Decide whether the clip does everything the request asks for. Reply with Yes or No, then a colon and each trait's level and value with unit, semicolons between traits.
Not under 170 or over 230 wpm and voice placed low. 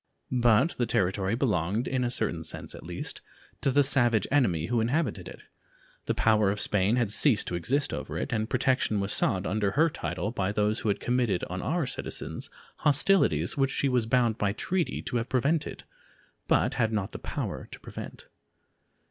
Yes: average, 185 wpm; low, 115 Hz